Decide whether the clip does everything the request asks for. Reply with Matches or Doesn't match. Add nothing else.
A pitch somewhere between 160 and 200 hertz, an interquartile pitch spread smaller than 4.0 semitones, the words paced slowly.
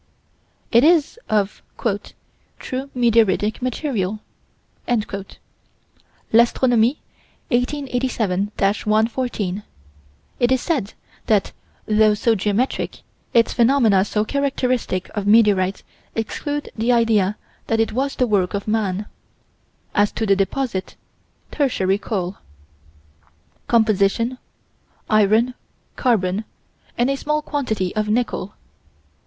Doesn't match